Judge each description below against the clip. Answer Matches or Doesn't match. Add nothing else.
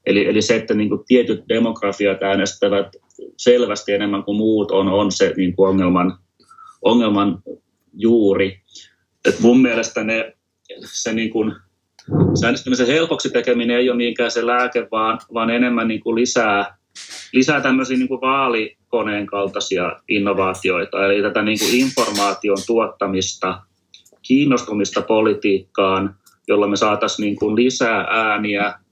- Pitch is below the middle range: Matches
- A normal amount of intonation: Matches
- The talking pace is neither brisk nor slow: Matches